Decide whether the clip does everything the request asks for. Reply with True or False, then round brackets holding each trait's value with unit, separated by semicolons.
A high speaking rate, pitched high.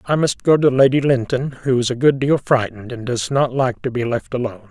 False (255 wpm; 130 Hz)